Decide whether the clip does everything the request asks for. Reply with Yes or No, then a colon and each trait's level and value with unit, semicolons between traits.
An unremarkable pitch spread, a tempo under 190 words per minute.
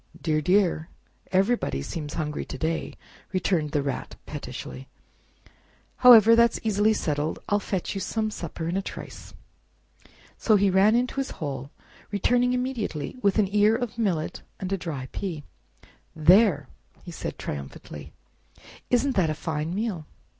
No: wide, 6.0 semitones; average, 140 wpm